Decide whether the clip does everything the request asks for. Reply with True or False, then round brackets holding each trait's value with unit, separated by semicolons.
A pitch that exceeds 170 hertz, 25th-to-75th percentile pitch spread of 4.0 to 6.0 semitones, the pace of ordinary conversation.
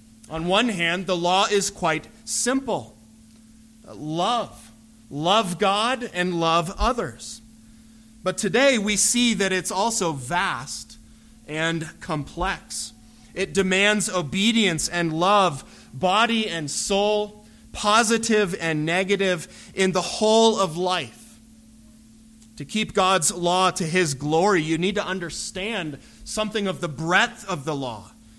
False (185 Hz; 5.2 semitones; 125 wpm)